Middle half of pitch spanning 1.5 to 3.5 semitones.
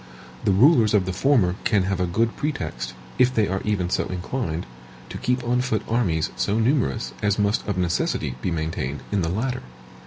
No: average, 5.0 semitones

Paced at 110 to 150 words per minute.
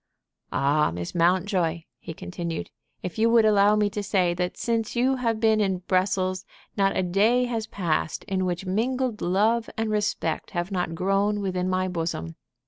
No: average, 170 wpm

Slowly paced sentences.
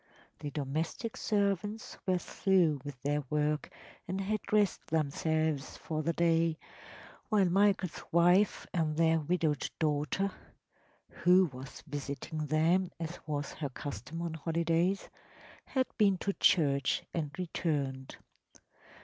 Yes: slow, 120 wpm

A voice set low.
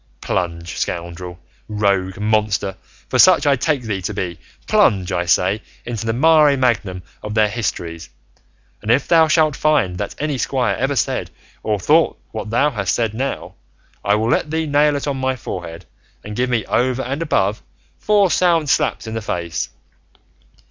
Yes: low, 115 Hz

